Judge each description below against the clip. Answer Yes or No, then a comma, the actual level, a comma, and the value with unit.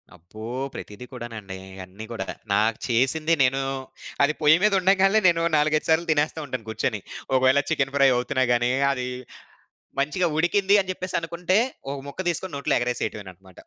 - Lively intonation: Yes, wide, 6.3 semitones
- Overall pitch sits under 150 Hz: Yes, medium, 140 Hz